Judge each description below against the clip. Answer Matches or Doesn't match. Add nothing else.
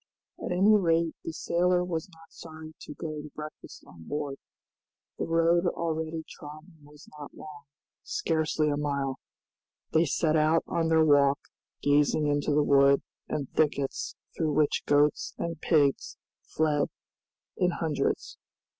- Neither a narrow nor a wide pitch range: Doesn't match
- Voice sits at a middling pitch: Matches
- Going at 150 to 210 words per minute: Doesn't match